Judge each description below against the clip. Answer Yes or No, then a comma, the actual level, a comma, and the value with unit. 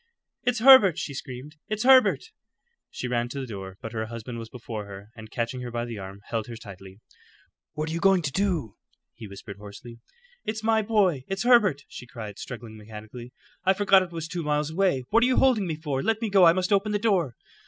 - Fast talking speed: Yes, fast, 215 wpm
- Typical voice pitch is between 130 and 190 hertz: Yes, medium, 140 Hz